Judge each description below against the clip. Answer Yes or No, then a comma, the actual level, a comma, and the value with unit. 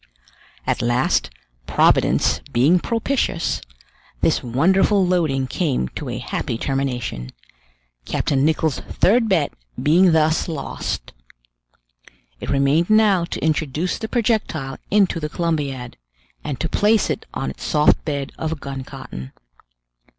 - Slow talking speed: Yes, slow, 120 wpm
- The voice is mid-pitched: Yes, medium, 155 Hz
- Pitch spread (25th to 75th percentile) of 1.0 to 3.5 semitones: No, average, 5.2 semitones